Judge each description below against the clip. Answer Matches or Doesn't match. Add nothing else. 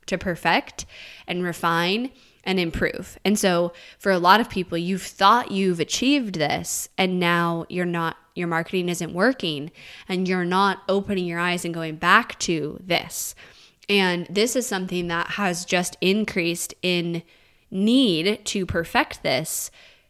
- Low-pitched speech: Doesn't match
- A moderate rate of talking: Matches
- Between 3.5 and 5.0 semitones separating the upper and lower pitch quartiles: Doesn't match